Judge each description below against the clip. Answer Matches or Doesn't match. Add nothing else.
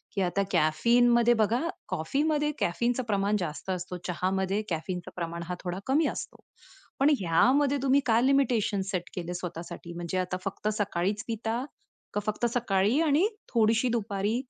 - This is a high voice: Matches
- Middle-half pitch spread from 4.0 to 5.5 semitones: Matches